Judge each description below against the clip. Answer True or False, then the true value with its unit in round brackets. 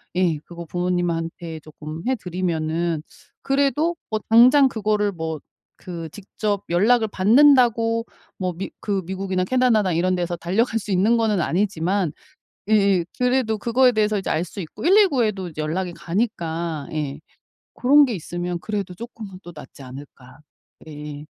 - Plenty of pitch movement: False (4.9 semitones)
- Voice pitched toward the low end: False (185 Hz)